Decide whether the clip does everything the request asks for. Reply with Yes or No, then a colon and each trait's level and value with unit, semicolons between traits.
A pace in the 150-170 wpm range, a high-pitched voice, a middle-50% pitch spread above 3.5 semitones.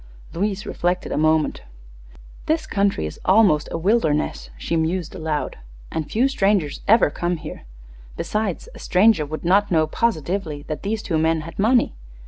No: average, 155 wpm; medium, 175 Hz; average, 4.7 semitones